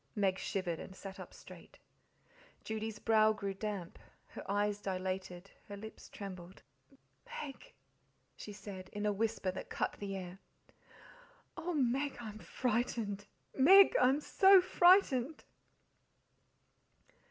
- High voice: Yes, high, 210 Hz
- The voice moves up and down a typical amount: Yes, average, 4.8 semitones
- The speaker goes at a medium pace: No, slow, 120 wpm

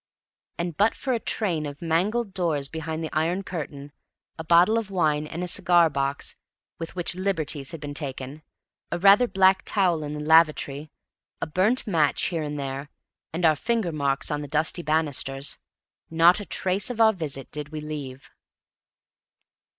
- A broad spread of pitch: No, average, 3.8 semitones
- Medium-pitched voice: Yes, medium, 160 Hz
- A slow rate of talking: No, average, 170 wpm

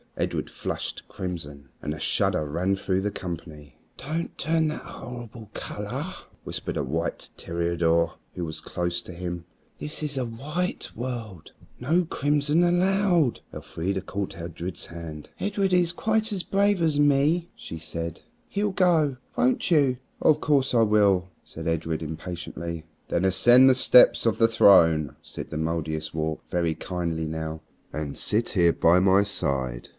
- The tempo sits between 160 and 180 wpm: No, average, 150 wpm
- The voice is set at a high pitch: No, very low, 95 Hz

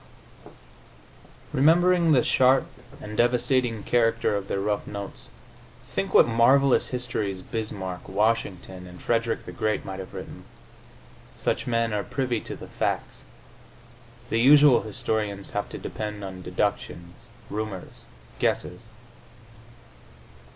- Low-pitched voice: Yes, low, 110 Hz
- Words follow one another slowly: Yes, slow, 115 wpm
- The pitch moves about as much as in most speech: Yes, average, 3.7 semitones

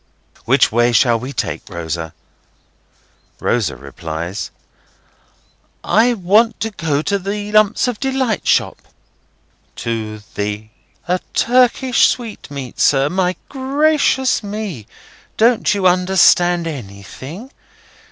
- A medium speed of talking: No, slow, 105 wpm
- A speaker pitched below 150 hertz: No, medium, 180 Hz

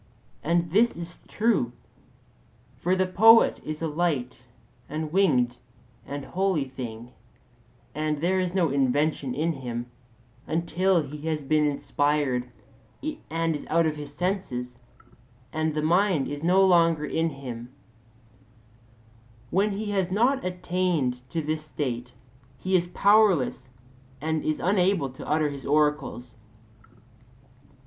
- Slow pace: Yes, slow, 125 wpm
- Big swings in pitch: No, average, 4.6 semitones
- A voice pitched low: No, medium, 155 Hz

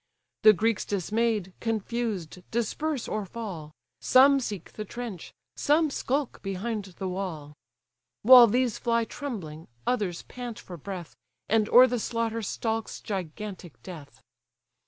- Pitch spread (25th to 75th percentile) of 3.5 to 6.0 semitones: Yes, average, 4.1 semitones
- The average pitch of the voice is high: Yes, high, 215 Hz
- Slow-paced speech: Yes, slow, 125 wpm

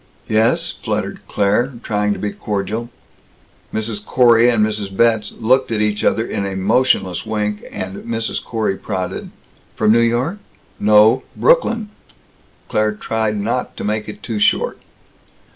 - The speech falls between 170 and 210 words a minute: No, average, 145 wpm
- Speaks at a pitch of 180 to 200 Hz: No, low, 110 Hz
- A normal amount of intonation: No, narrow, 2.1 semitones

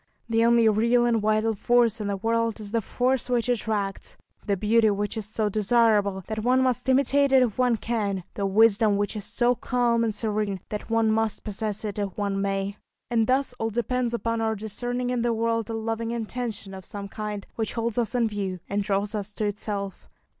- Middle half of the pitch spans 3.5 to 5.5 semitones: No, narrow, 2.4 semitones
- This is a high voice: Yes, high, 220 Hz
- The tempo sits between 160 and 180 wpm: No, fast, 205 wpm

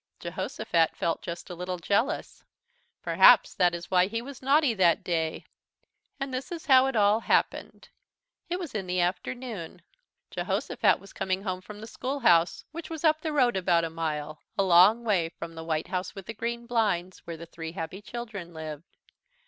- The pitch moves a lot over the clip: Yes, wide, 6.0 semitones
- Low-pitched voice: No, high, 190 Hz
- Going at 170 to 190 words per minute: Yes, average, 180 wpm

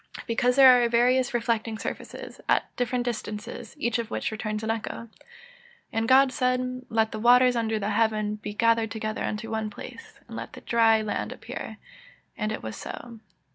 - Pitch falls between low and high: No, high, 230 Hz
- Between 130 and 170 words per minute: No, average, 185 wpm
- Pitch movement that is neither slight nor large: No, narrow, 2.2 semitones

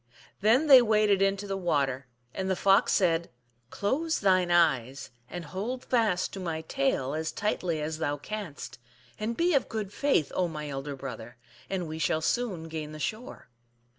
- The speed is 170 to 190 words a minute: Yes, average, 175 wpm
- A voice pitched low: No, medium, 180 Hz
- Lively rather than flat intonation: Yes, wide, 5.7 semitones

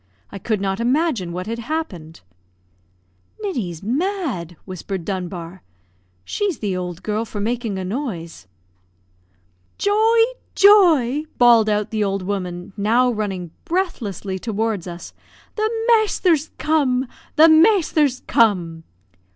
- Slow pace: Yes, slow, 115 wpm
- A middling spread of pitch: No, wide, 8.5 semitones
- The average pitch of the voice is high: Yes, high, 220 Hz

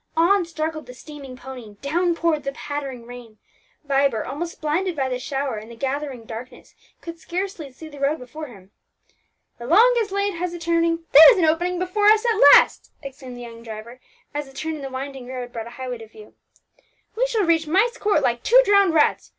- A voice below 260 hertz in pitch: No, very high, 290 Hz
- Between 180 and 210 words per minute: Yes, fast, 205 wpm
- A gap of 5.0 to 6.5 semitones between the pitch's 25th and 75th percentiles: Yes, wide, 5.4 semitones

